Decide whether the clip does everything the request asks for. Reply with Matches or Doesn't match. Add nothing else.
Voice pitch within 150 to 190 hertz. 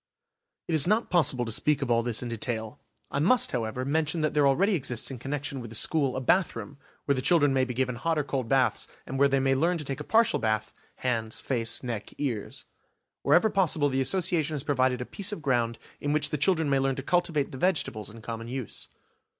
Doesn't match